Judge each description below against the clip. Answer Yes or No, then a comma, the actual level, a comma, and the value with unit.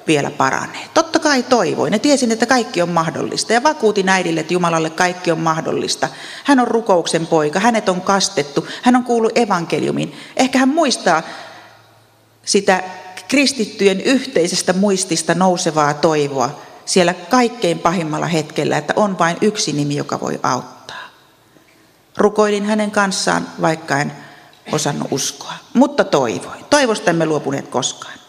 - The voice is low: No, high, 190 Hz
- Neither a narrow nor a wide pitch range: No, wide, 6.0 semitones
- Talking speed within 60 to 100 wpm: No, average, 135 wpm